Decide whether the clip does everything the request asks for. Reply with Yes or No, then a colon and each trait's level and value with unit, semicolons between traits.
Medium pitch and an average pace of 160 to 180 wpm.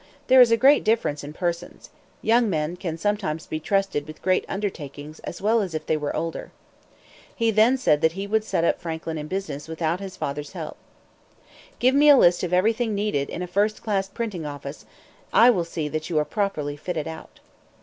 No: medium, 180 Hz; average, 200 wpm